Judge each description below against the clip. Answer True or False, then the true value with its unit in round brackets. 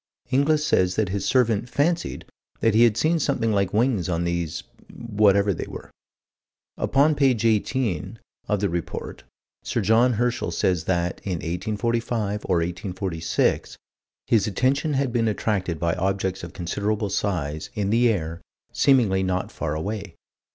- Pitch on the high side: False (105 Hz)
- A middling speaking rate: True (145 wpm)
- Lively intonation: False (4.7 semitones)